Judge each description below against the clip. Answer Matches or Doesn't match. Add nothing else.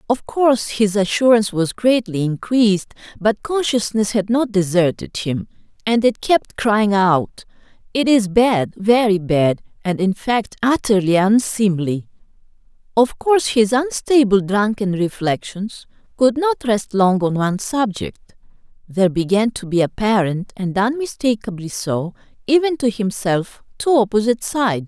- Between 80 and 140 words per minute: Matches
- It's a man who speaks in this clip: Doesn't match